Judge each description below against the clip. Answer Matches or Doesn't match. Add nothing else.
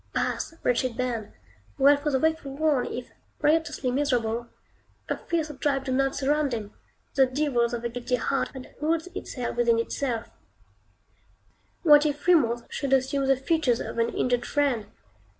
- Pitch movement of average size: Matches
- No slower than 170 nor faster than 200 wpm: Doesn't match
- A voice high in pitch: Matches